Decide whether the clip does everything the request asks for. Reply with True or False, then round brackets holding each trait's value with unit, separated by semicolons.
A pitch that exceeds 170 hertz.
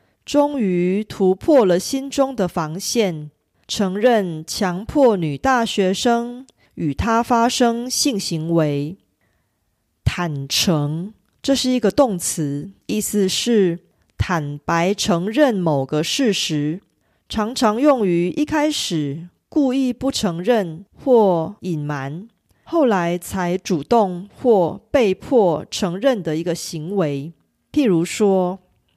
True (190 Hz)